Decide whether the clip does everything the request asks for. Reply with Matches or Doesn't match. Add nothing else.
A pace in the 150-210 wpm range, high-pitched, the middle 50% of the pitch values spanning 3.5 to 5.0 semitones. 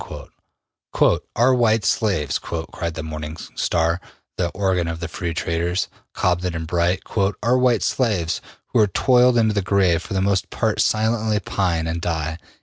Doesn't match